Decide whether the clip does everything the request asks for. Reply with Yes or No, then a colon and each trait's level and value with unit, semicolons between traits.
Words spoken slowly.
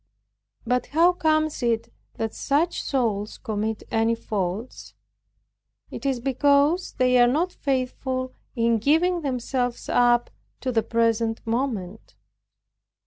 Yes: slow, 105 wpm